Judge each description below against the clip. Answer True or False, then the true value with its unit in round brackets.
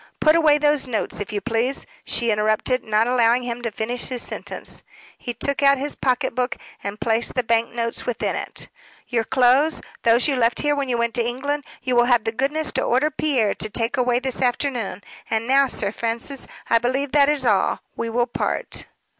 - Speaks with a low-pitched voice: False (245 Hz)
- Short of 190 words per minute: False (205 wpm)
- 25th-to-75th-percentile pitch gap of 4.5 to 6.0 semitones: False (3.0 semitones)